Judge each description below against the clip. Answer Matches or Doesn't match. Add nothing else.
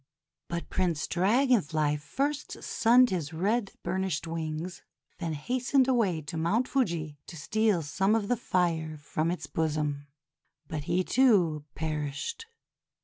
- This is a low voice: Doesn't match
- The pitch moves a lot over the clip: Matches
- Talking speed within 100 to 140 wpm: Matches